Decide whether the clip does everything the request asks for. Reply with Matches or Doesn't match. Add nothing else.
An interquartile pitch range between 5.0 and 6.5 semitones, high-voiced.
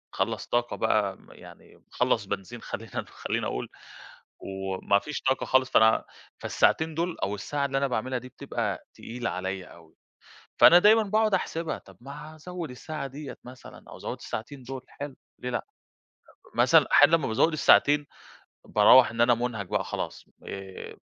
Doesn't match